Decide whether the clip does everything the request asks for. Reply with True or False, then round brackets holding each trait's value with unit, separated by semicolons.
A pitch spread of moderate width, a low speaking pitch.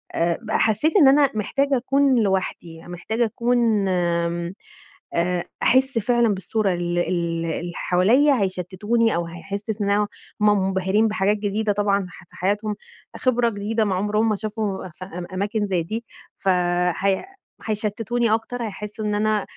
False (3.4 semitones; 205 Hz)